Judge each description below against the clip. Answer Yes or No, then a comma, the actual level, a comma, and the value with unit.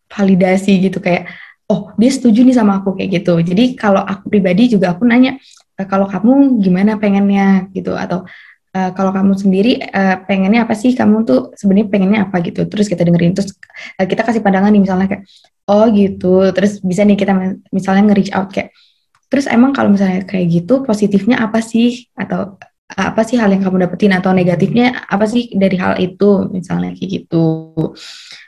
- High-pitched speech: Yes, high, 195 Hz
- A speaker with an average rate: No, fast, 175 wpm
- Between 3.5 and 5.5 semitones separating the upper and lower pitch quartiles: No, average, 2.7 semitones